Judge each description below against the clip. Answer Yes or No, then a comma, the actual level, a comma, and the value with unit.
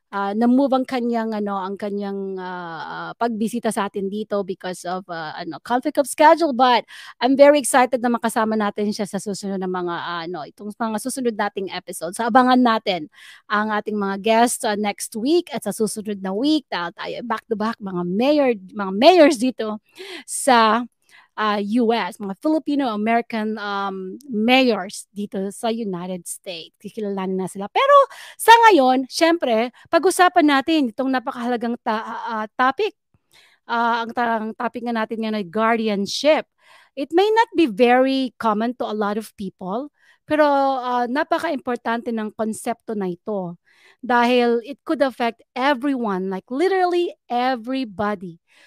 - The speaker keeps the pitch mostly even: No, average, 4.3 semitones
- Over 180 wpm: No, average, 155 wpm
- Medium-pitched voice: No, high, 230 Hz